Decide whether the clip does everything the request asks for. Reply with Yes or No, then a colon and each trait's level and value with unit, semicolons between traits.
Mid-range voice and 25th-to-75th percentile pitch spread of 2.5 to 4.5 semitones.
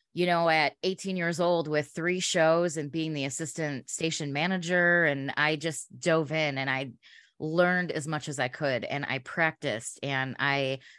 Yes: medium, 155 Hz; average, 3.4 semitones